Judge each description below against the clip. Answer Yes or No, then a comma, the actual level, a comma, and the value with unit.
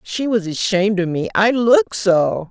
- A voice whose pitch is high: Yes, high, 205 Hz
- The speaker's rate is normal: Yes, average, 190 wpm